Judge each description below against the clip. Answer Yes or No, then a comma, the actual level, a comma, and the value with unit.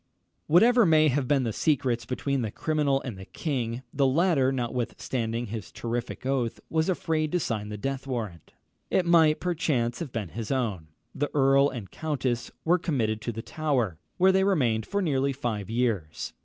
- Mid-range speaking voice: No, low, 130 Hz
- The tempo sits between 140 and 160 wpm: No, average, 180 wpm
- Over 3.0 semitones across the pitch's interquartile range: Yes, average, 5.1 semitones